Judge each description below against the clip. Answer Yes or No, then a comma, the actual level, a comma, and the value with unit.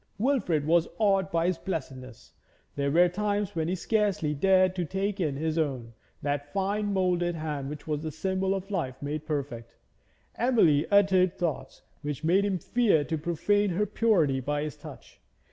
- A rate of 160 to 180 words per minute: Yes, average, 170 wpm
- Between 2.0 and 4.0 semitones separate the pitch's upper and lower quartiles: No, average, 4.7 semitones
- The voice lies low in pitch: No, medium, 170 Hz